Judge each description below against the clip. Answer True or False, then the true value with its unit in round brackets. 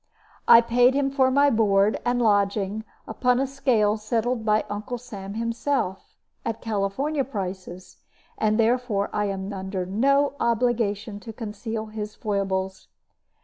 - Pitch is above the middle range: True (220 Hz)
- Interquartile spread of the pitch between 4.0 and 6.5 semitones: False (3.5 semitones)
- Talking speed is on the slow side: True (130 wpm)